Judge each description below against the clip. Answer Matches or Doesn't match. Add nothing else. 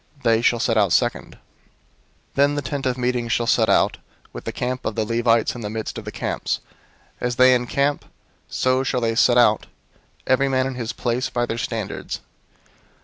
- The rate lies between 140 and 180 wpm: Doesn't match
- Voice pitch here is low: Matches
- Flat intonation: Matches